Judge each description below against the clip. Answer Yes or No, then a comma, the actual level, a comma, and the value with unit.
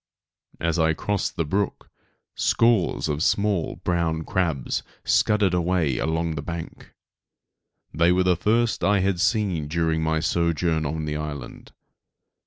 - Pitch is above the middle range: No, very low, 85 Hz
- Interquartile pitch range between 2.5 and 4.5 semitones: Yes, average, 2.9 semitones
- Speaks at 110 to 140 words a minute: Yes, slow, 135 wpm